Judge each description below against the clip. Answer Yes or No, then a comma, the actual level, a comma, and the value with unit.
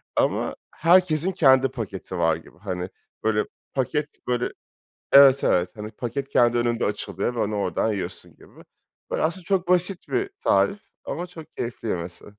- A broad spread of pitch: Yes, wide, 7.6 semitones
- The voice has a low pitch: Yes, low, 125 Hz